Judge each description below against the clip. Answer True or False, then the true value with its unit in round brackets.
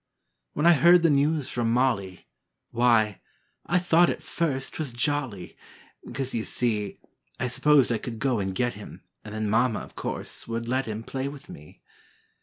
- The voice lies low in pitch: True (125 Hz)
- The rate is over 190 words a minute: False (175 wpm)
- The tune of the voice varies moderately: True (4.6 semitones)